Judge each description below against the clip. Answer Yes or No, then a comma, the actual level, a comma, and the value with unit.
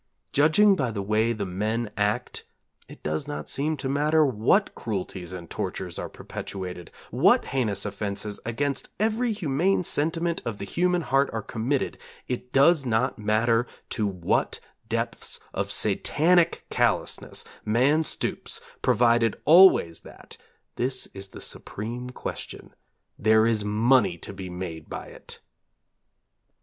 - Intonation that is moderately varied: No, wide, 5.8 semitones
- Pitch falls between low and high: No, low, 115 Hz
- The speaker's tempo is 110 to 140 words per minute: Yes, slow, 135 wpm